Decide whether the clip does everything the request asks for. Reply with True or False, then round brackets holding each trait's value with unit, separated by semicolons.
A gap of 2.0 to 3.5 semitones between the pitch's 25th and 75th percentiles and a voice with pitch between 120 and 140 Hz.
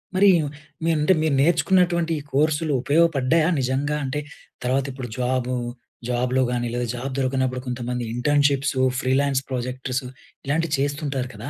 True (2.8 semitones; 135 Hz)